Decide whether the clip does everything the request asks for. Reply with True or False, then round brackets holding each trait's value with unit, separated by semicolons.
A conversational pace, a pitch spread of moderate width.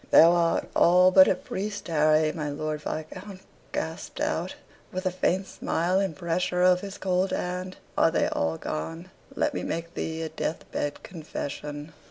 True (170 wpm; 3.0 semitones)